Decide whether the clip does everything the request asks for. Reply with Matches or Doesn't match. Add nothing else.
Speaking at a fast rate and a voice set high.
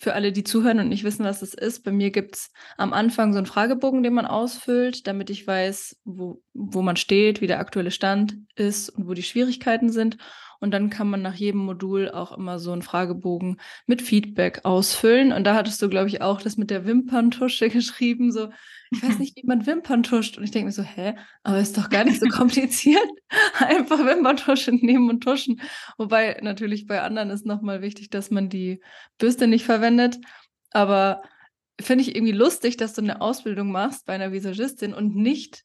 Matches